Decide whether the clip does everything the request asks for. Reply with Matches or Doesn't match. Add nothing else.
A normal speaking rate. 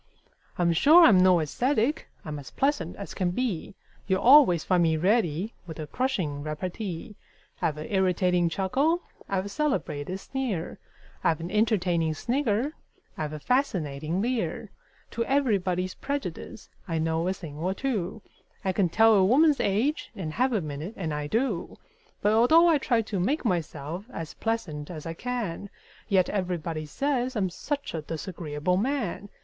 Matches